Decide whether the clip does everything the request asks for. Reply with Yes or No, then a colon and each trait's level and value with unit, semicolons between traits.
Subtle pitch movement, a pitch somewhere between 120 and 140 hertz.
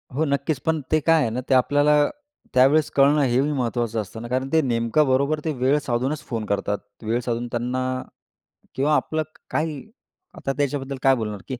No: average, 3.7 semitones; low, 135 Hz